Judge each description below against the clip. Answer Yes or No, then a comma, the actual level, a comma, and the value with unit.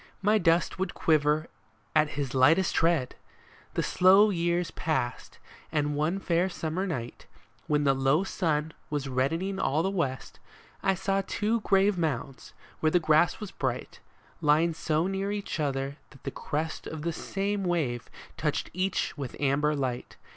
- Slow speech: No, average, 160 wpm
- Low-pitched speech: No, medium, 160 Hz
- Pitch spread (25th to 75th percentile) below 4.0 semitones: No, average, 4.5 semitones